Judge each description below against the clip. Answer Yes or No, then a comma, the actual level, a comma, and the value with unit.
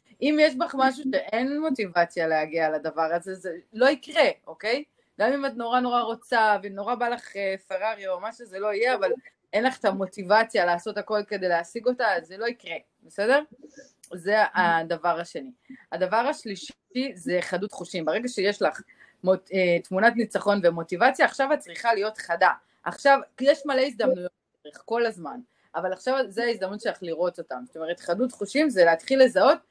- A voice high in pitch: Yes, high, 220 Hz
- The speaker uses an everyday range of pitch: No, wide, 6.5 semitones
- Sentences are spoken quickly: Yes, fast, 170 wpm